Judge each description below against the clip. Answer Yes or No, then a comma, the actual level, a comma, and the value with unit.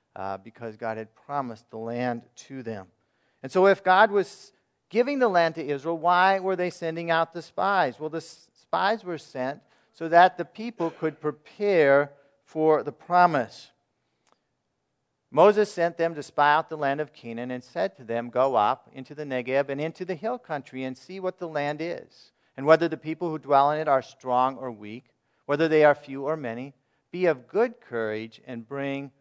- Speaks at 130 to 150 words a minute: No, average, 195 wpm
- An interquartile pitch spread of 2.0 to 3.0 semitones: No, average, 4.7 semitones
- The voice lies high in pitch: No, medium, 150 Hz